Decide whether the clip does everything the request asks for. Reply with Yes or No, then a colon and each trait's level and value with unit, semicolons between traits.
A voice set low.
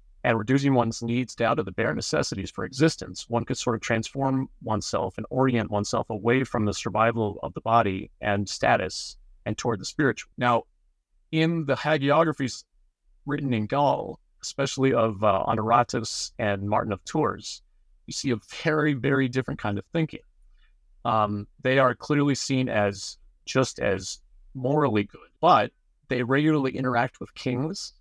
Yes: low, 120 Hz